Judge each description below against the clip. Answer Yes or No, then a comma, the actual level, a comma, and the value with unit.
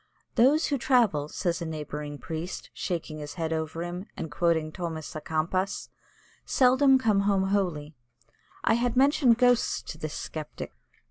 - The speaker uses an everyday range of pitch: No, wide, 6.7 semitones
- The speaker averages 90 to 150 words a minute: Yes, average, 145 wpm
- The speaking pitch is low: No, medium, 175 Hz